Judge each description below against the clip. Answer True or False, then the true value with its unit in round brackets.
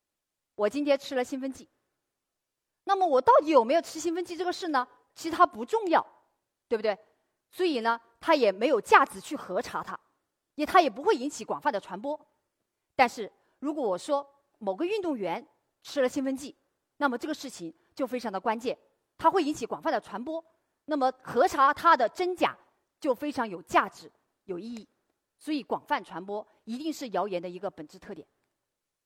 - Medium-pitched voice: False (280 Hz)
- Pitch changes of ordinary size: False (5.9 semitones)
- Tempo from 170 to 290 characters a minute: True (270 characters per minute)